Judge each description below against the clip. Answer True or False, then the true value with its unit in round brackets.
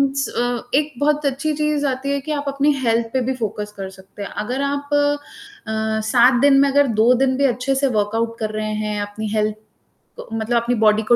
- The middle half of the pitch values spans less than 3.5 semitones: False (4.4 semitones)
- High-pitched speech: True (245 Hz)